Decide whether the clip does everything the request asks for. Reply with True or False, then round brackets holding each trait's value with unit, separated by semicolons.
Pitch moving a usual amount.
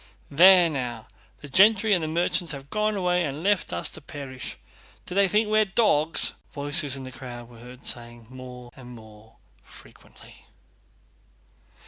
False (6.8 semitones)